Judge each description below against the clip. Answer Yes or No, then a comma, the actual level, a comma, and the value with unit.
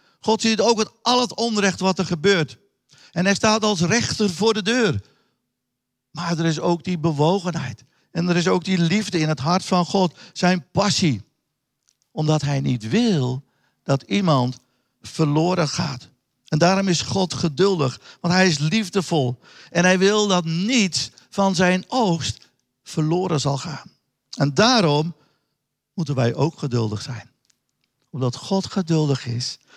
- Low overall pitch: No, medium, 165 Hz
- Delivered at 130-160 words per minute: Yes, average, 155 wpm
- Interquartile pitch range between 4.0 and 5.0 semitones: No, wide, 5.6 semitones